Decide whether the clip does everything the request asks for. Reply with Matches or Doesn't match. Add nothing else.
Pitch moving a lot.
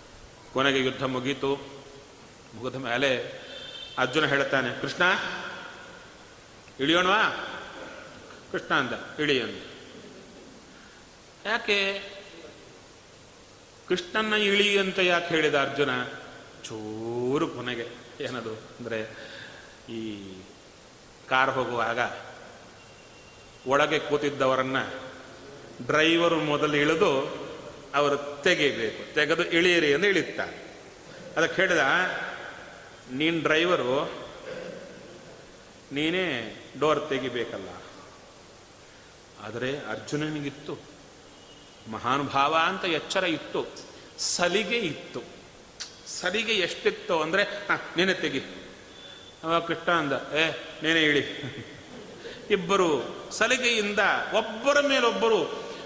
Matches